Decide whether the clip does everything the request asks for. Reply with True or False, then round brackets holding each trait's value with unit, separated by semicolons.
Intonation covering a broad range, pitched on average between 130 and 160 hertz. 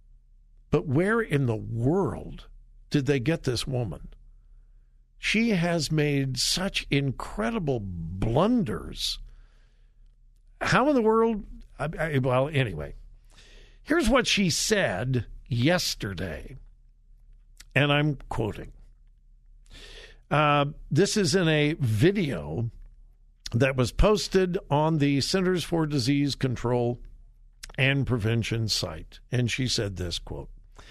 True (6.3 semitones; 135 Hz)